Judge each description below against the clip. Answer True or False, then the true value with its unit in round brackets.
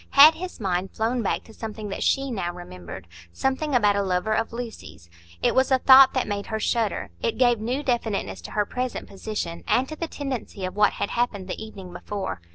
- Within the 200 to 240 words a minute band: True (205 wpm)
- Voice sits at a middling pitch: False (220 Hz)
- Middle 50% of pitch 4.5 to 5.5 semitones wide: True (4.9 semitones)